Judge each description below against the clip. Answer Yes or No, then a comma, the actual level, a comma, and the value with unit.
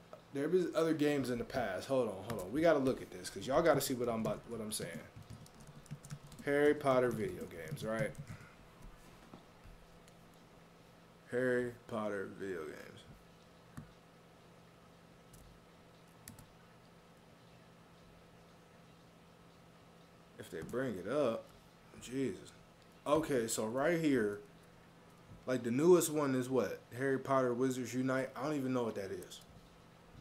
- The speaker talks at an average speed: No, slow, 125 wpm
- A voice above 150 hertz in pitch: No, low, 130 Hz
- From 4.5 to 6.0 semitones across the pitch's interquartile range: No, average, 3.3 semitones